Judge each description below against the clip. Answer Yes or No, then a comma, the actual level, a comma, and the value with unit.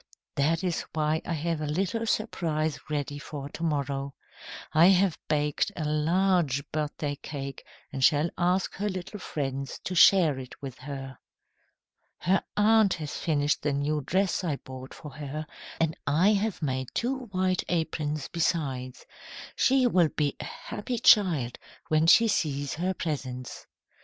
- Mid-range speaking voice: Yes, medium, 155 Hz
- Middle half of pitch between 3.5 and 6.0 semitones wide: Yes, average, 4.3 semitones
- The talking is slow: No, average, 150 wpm